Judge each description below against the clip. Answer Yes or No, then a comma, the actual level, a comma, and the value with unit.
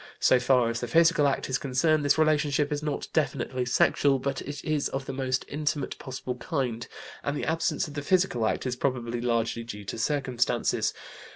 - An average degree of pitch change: Yes, average, 3.1 semitones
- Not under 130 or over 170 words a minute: No, average, 190 wpm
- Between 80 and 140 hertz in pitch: Yes, low, 135 Hz